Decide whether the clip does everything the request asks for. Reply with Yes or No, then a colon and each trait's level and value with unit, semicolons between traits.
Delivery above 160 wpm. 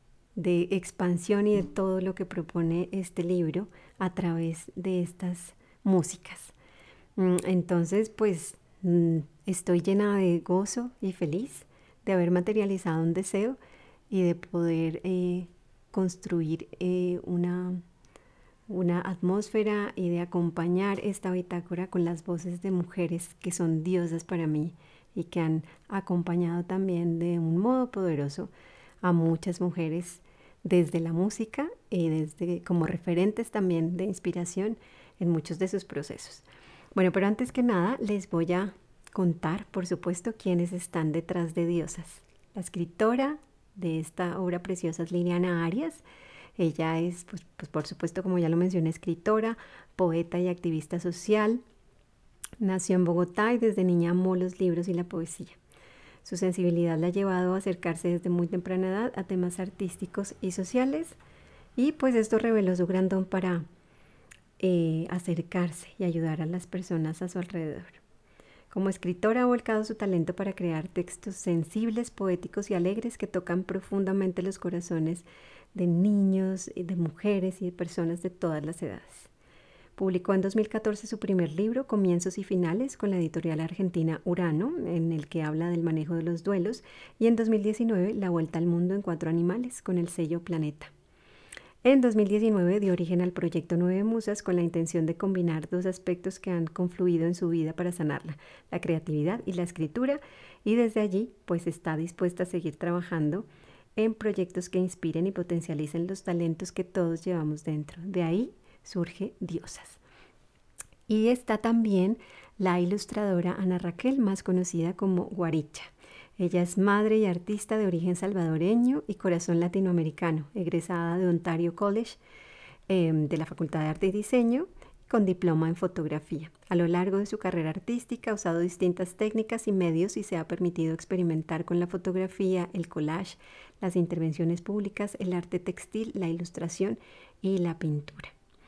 No: average, 155 wpm